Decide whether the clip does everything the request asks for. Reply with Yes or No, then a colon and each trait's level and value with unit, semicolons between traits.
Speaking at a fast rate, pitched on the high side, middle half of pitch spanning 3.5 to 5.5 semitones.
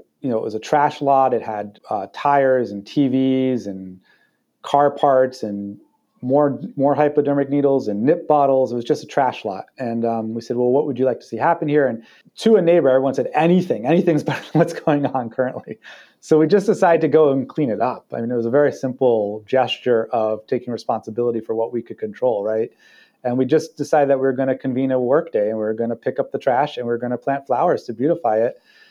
No: fast, 240 wpm; low, 130 Hz; average, 3.8 semitones